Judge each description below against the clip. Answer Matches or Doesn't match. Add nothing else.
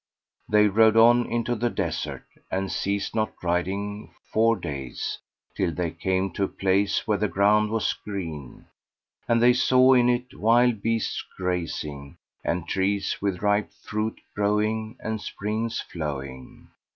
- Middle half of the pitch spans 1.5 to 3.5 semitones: Matches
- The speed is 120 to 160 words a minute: Matches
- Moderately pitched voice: Doesn't match